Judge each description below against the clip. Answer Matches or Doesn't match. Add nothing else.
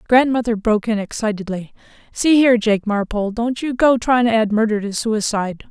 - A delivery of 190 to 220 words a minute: Doesn't match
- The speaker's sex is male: Doesn't match